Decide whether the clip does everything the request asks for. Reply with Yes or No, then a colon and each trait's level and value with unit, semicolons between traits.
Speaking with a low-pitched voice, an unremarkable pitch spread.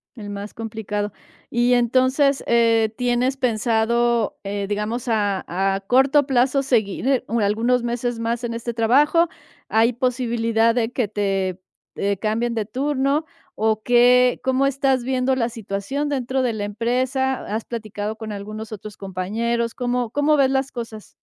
No: high, 235 Hz; average, 3.0 semitones